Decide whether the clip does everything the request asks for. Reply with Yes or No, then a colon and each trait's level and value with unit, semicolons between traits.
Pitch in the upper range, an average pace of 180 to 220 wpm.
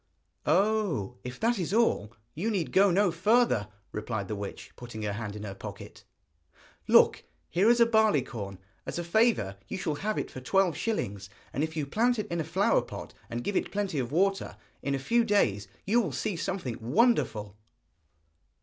No: medium, 165 Hz; average, 190 wpm